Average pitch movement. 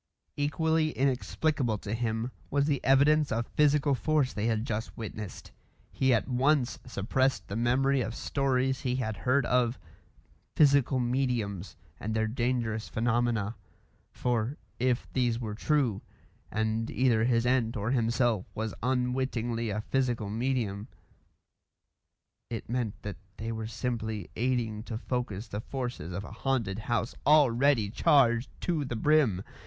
Yes: average, 3.2 semitones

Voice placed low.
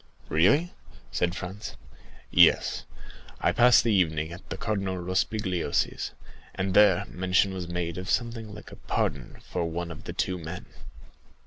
Yes: very low, 95 Hz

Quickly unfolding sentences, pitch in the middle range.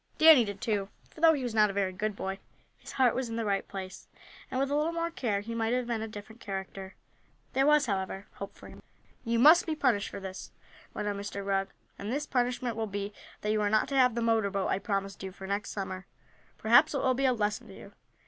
No: fast, 250 wpm; high, 215 Hz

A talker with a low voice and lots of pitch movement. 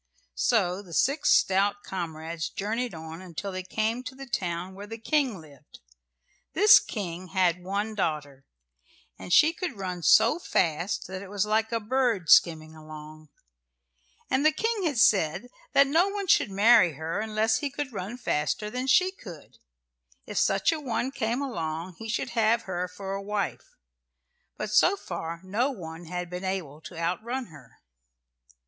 No: high, 195 Hz; wide, 6.1 semitones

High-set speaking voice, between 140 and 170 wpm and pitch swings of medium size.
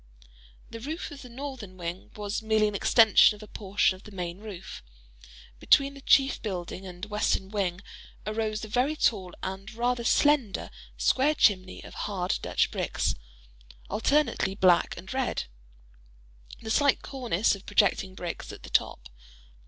Yes: high, 210 Hz; average, 150 wpm; average, 4.5 semitones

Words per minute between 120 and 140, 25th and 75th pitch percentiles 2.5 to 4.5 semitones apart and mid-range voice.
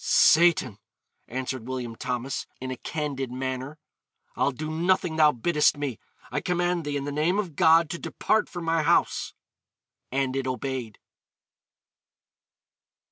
Yes: slow, 135 wpm; average, 4.2 semitones; medium, 145 Hz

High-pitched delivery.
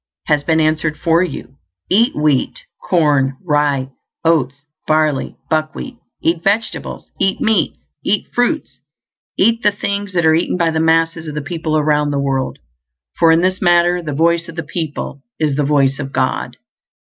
No: medium, 160 Hz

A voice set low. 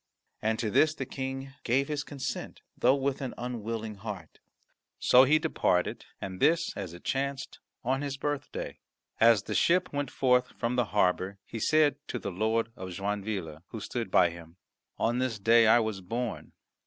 Yes: low, 115 Hz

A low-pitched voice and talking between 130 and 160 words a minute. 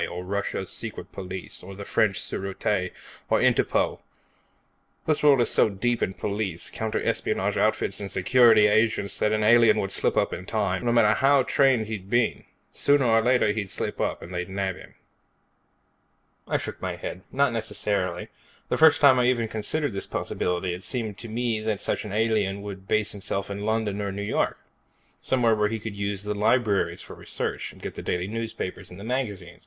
No: low, 105 Hz; average, 190 wpm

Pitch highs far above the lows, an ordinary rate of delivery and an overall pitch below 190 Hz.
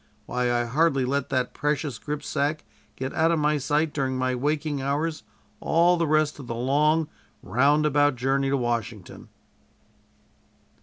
No: average, 2.9 semitones; average, 145 wpm; medium, 140 Hz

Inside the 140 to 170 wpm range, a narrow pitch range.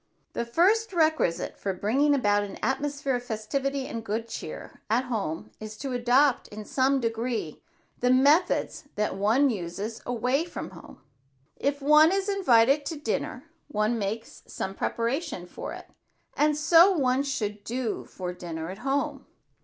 No: average, 155 wpm; average, 5.1 semitones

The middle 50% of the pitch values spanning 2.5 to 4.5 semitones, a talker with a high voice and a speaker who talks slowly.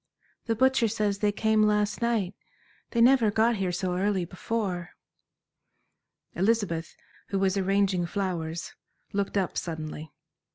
Yes: average, 3.4 semitones; high, 200 Hz; slow, 125 wpm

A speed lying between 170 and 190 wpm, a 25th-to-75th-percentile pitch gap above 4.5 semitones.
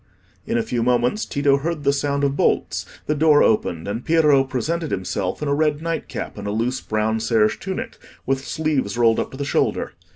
No: fast, 205 wpm; average, 5.0 semitones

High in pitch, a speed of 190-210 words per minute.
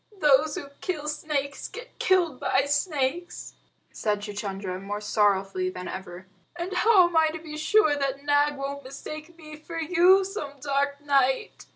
No: very high, 290 Hz; average, 160 wpm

